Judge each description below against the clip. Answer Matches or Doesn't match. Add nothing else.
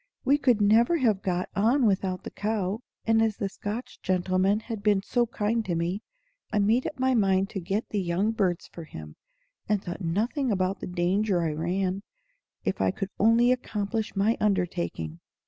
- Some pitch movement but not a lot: Matches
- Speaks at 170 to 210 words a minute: Matches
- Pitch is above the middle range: Matches